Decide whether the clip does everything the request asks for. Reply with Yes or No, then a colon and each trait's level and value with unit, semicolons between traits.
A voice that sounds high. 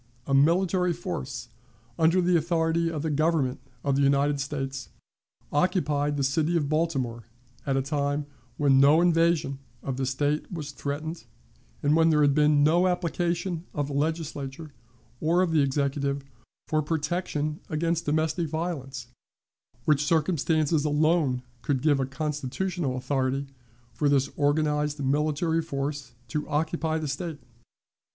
No: medium, 150 Hz